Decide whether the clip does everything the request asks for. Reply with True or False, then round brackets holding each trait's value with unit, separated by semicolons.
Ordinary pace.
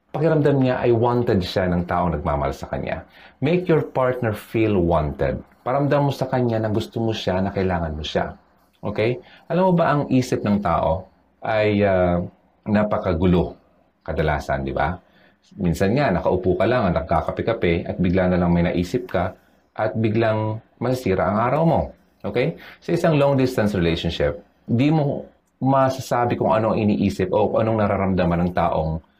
False (160 wpm)